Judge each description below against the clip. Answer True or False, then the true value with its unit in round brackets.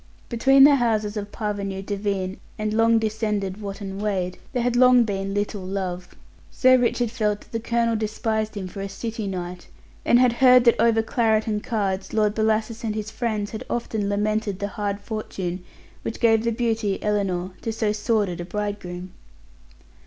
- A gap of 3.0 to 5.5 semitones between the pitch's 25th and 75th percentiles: False (2.4 semitones)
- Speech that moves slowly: False (175 wpm)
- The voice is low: False (215 Hz)